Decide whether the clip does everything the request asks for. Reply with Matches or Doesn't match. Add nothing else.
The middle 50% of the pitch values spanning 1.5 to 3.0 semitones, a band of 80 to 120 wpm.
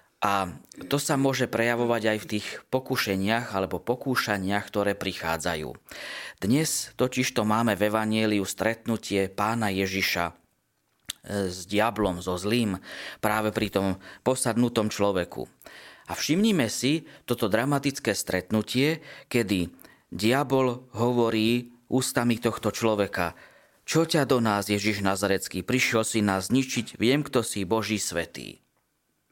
Doesn't match